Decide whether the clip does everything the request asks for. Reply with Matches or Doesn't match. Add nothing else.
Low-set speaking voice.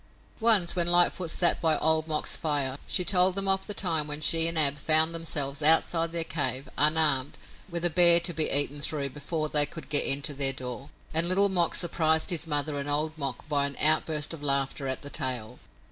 Doesn't match